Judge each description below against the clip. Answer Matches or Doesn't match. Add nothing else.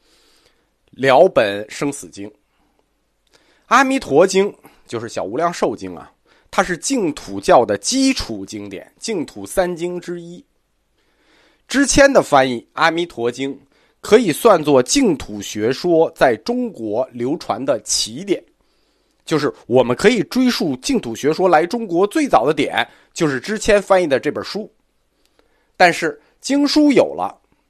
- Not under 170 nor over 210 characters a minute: Matches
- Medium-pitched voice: Matches